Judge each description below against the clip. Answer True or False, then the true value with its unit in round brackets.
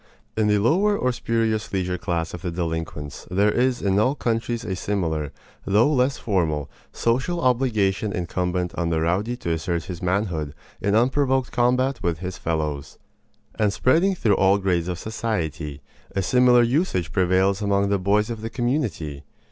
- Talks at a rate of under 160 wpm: False (165 wpm)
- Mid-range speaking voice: False (100 Hz)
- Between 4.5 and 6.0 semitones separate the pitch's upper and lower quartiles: True (5.6 semitones)